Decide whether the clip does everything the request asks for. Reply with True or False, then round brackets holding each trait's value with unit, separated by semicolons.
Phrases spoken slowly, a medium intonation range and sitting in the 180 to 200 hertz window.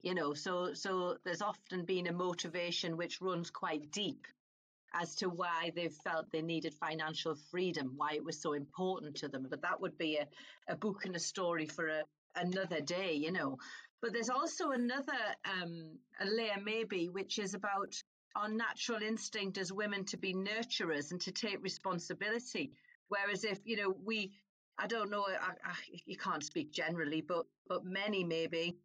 False (180 wpm; 3.7 semitones; 185 Hz)